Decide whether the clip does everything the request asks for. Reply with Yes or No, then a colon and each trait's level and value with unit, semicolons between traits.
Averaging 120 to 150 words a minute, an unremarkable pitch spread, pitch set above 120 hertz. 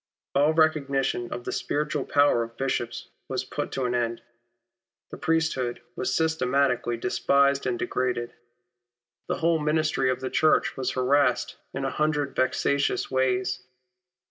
Yes: average, 140 wpm; average, 3.0 semitones; low, 135 Hz